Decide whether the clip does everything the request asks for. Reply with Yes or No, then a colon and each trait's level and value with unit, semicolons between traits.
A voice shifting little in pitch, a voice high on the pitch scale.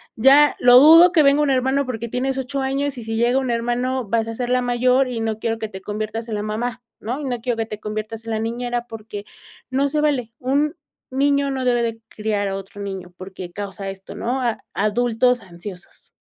No: average, 3.4 semitones; high, 240 Hz